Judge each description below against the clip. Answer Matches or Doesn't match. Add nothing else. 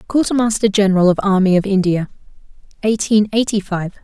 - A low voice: Doesn't match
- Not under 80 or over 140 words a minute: Matches